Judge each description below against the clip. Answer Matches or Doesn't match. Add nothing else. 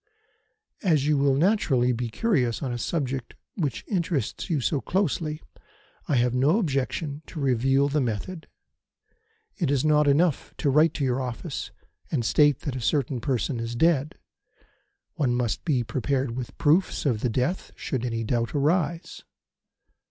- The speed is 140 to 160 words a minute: Matches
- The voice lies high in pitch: Doesn't match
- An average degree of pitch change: Matches